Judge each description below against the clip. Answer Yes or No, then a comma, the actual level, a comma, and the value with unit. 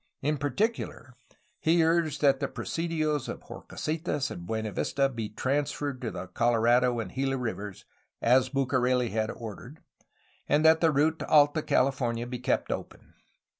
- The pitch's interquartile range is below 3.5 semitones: No, average, 4.0 semitones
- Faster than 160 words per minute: No, average, 145 wpm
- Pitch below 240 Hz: Yes, low, 135 Hz